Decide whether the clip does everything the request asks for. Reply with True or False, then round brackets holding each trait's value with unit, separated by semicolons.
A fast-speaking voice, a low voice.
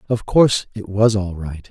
True (210 wpm; 100 Hz)